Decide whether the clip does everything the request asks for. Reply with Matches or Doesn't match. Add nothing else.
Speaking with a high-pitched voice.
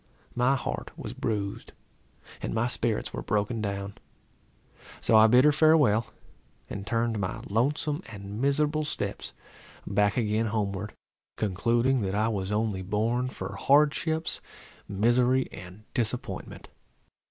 Doesn't match